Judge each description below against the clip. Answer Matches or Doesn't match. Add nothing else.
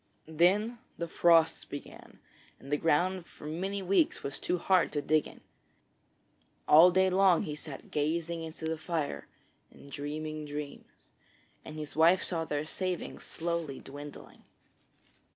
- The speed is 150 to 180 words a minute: Doesn't match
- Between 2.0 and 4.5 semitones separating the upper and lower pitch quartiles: Matches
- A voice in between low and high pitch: Matches